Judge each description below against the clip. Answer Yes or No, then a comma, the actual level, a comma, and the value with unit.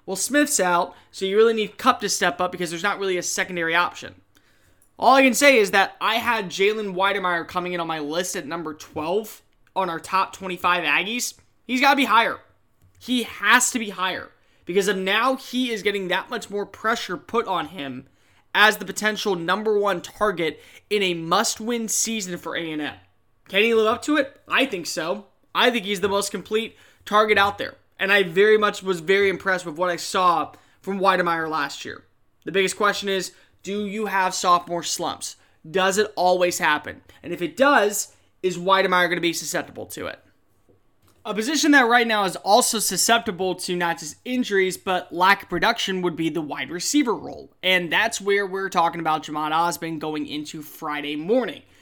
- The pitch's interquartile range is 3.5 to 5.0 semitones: Yes, average, 3.9 semitones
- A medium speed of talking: Yes, average, 195 wpm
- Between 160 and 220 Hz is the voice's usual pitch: Yes, high, 190 Hz